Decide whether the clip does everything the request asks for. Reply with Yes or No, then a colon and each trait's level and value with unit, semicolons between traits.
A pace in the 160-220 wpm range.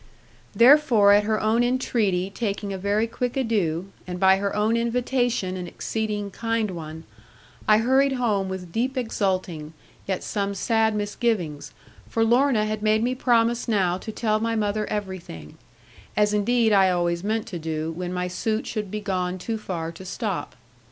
Yes: average, 165 wpm